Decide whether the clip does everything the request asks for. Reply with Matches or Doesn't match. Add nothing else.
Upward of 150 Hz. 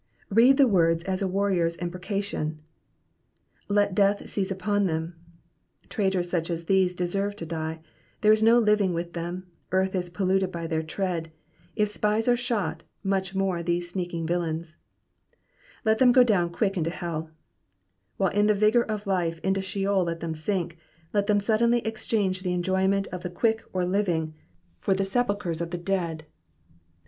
Matches